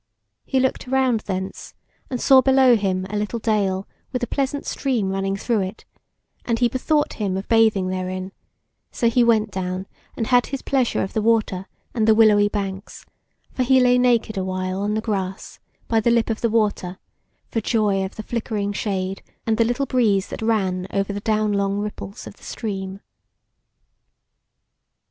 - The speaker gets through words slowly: No, average, 180 wpm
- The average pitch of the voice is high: Yes, high, 215 Hz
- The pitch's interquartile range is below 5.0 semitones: Yes, average, 3.5 semitones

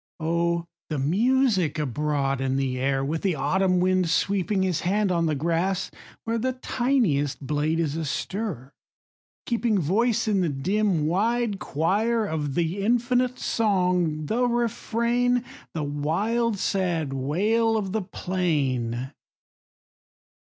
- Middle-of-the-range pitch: Yes, medium, 180 Hz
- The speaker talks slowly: Yes, slow, 125 wpm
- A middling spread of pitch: No, wide, 6.6 semitones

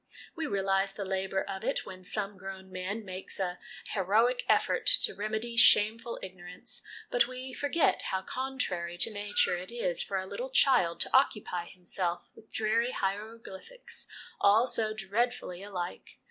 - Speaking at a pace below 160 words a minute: Yes, average, 150 wpm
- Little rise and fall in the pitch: No, average, 3.8 semitones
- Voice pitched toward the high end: Yes, high, 200 Hz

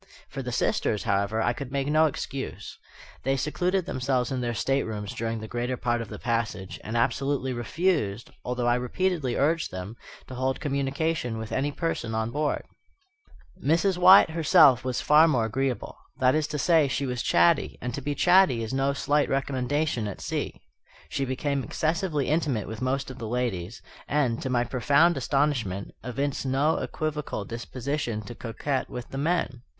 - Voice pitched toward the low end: Yes, low, 130 Hz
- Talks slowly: No, average, 170 wpm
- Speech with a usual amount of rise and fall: Yes, average, 3.9 semitones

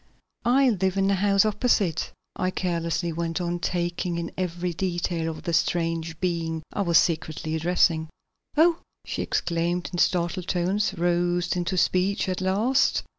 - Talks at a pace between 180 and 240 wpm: No, average, 150 wpm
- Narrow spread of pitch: Yes, narrow, 2.1 semitones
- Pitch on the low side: No, medium, 175 Hz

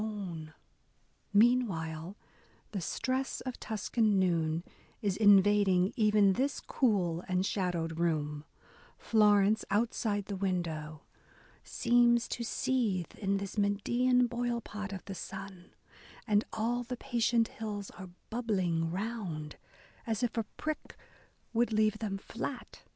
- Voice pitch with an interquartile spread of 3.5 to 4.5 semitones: Yes, average, 4.2 semitones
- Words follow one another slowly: Yes, slow, 120 wpm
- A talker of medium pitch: No, high, 205 Hz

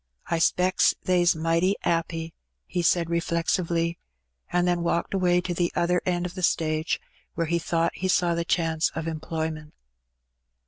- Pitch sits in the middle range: Yes, medium, 170 Hz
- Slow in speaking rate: No, average, 165 wpm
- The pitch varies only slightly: Yes, narrow, 1.3 semitones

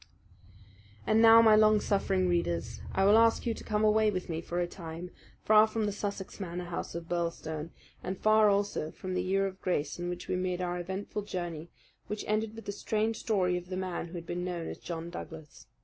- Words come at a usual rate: No, fast, 215 wpm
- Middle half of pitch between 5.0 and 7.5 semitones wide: No, average, 3.5 semitones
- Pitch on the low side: No, medium, 185 Hz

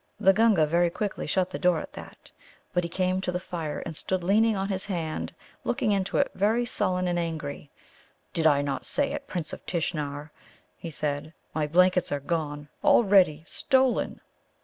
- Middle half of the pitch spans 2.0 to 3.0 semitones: No, average, 3.7 semitones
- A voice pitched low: No, medium, 180 Hz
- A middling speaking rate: Yes, average, 180 wpm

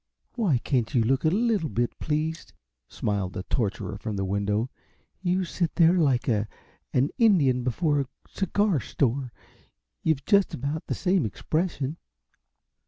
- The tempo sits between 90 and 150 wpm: Yes, average, 145 wpm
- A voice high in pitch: No, medium, 140 Hz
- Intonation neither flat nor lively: No, wide, 6.6 semitones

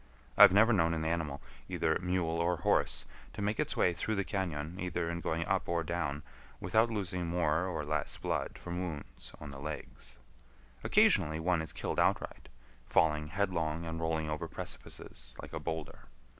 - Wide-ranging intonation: No, narrow, 2.6 semitones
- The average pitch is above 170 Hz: No, very low, 85 Hz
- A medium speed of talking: Yes, average, 170 wpm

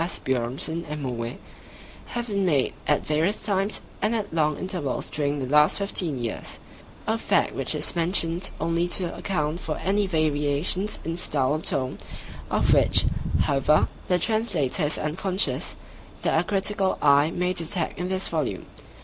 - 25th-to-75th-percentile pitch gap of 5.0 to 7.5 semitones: No, average, 4.3 semitones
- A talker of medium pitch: Yes, medium, 165 Hz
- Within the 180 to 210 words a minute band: No, average, 150 wpm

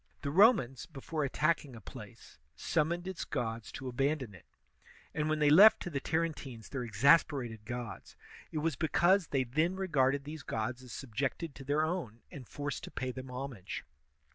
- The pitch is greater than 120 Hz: Yes, medium, 140 Hz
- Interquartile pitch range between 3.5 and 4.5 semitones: Yes, average, 4.2 semitones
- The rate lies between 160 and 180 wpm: Yes, average, 175 wpm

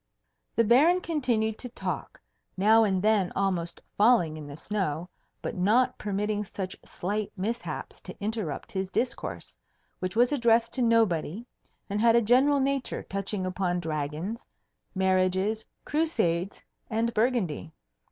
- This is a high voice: Yes, high, 210 Hz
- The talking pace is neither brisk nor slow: No, slow, 130 wpm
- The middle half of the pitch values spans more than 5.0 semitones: No, average, 4.1 semitones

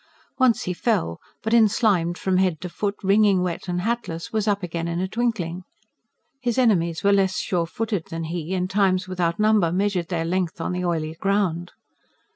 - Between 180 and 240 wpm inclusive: Yes, average, 185 wpm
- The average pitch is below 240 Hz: Yes, medium, 185 Hz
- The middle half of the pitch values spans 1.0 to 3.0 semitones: No, average, 3.4 semitones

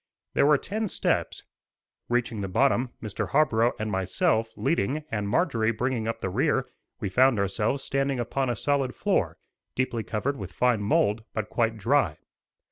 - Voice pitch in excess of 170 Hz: No, low, 115 Hz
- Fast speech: No, average, 160 wpm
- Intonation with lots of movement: No, average, 4.2 semitones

